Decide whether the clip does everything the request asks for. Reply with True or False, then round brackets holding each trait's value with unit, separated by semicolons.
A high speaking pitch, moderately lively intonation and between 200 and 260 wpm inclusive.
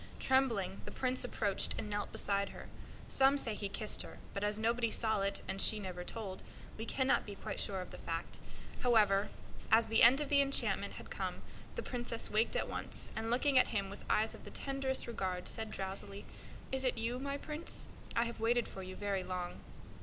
True (220 Hz; 4.1 semitones; 205 wpm)